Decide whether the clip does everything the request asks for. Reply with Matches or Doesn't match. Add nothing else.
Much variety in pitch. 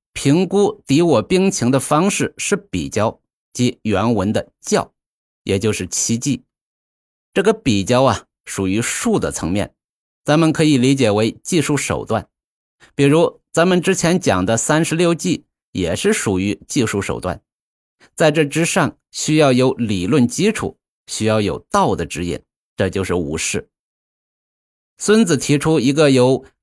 Matches